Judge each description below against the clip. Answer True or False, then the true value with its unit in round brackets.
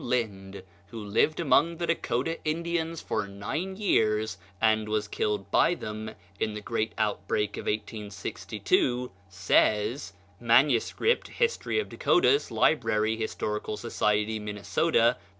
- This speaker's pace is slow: True (120 wpm)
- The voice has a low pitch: True (110 Hz)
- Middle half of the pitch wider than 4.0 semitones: True (5.5 semitones)